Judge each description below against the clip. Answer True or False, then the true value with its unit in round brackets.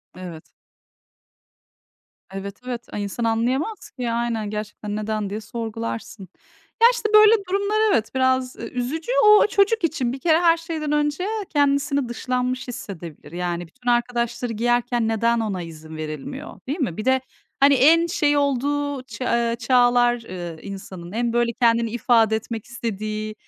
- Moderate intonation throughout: True (4.7 semitones)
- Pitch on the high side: True (240 Hz)